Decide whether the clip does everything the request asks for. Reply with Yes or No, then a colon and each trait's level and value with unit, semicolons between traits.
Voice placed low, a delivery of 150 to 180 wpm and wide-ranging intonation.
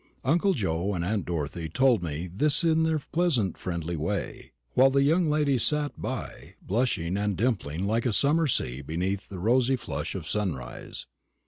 Yes: low, 105 Hz; average, 165 wpm; wide, 8.3 semitones